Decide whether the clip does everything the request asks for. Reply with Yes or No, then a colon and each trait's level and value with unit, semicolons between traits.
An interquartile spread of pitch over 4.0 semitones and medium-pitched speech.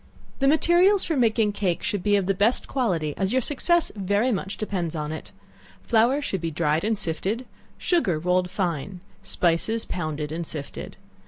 No: wide, 5.6 semitones; high, 195 Hz